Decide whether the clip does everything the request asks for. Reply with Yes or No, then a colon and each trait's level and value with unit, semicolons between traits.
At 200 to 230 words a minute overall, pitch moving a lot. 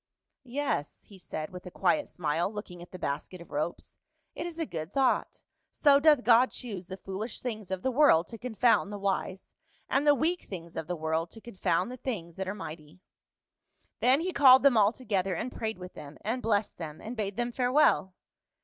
Yes: fast, 205 wpm; wide, 6.1 semitones